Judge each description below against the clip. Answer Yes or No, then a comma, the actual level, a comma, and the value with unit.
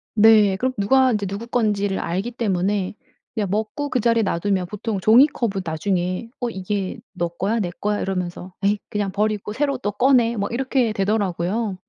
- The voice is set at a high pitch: Yes, high, 205 Hz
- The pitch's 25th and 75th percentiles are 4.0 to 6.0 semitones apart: No, average, 3.2 semitones